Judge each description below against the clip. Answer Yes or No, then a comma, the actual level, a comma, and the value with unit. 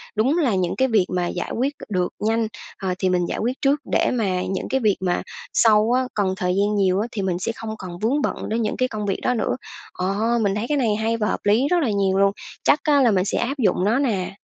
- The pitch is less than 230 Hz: Yes, high, 215 Hz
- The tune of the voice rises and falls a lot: No, average, 4.1 semitones